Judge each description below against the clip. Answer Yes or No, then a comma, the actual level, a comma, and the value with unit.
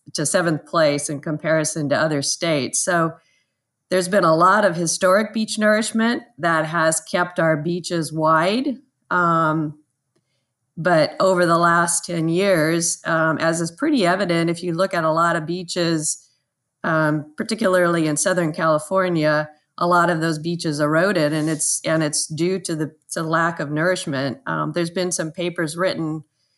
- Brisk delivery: No, average, 165 wpm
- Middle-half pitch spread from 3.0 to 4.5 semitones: No, narrow, 2.6 semitones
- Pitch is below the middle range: No, medium, 165 Hz